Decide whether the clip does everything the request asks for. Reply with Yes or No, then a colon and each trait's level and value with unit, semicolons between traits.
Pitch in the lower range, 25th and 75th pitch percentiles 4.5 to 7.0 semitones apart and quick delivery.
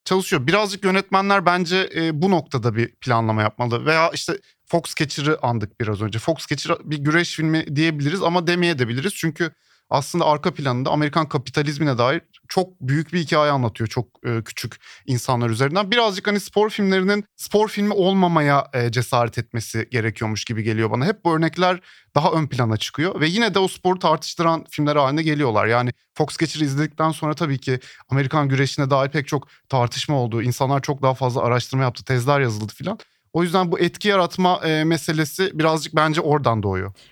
No: medium, 150 Hz; wide, 5.4 semitones; fast, 170 wpm